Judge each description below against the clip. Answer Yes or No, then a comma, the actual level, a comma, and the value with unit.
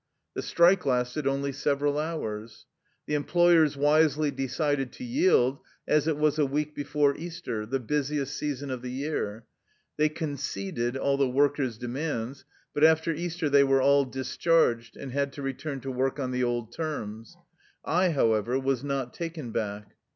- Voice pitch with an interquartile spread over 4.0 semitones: No, average, 3.2 semitones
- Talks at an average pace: Yes, average, 160 wpm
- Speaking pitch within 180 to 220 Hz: No, medium, 140 Hz